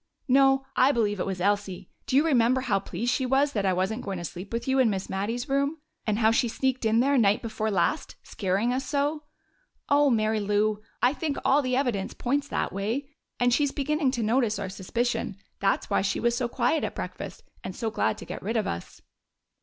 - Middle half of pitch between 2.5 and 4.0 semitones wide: No, average, 4.7 semitones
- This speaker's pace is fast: Yes, fast, 215 wpm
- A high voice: Yes, high, 235 Hz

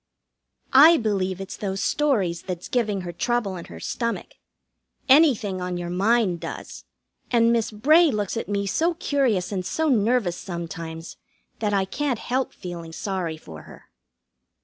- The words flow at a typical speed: Yes, average, 150 wpm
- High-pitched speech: Yes, high, 205 Hz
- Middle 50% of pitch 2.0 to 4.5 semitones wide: No, wide, 5.4 semitones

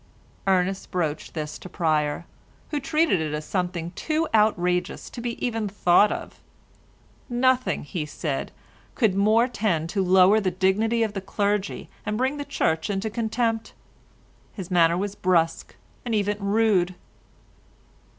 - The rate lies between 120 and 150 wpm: Yes, average, 140 wpm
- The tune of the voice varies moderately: Yes, average, 4.1 semitones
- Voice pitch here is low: No, high, 200 Hz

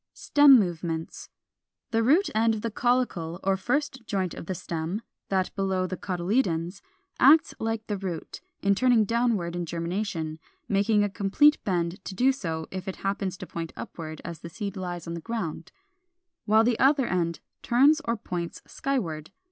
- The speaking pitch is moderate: No, high, 195 Hz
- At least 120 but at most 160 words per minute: No, average, 170 wpm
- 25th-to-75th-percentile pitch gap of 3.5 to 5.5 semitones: Yes, average, 5.2 semitones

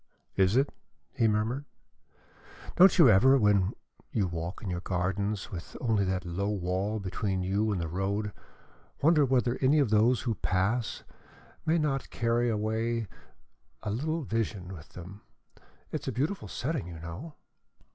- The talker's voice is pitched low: Yes, low, 105 Hz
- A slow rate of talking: No, average, 155 wpm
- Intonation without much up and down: No, average, 4.8 semitones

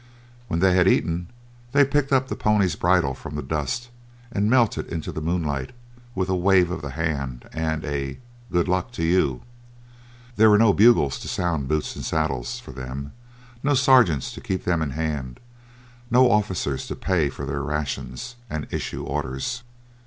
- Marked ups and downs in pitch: Yes, wide, 6.3 semitones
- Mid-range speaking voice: No, very low, 85 Hz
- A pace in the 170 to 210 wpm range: Yes, average, 175 wpm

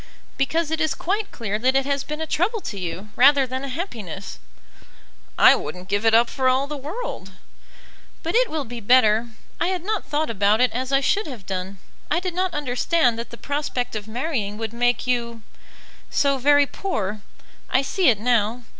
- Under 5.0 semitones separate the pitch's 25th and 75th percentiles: No, average, 5.3 semitones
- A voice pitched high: Yes, very high, 255 Hz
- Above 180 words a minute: Yes, average, 195 wpm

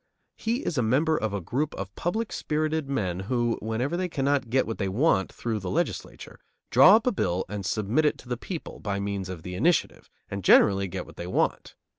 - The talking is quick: Yes, fast, 215 wpm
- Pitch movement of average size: No, wide, 7.8 semitones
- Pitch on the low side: Yes, low, 115 Hz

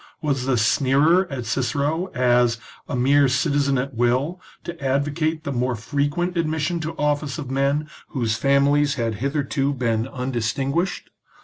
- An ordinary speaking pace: Yes, average, 145 wpm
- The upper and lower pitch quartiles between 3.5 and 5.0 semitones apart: No, average, 3.0 semitones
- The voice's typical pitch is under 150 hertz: Yes, medium, 140 Hz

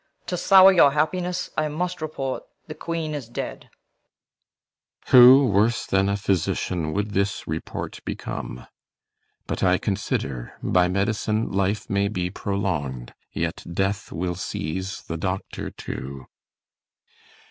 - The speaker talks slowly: Yes, slow, 125 wpm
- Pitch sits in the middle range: No, low, 100 Hz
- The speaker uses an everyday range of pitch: No, wide, 7.2 semitones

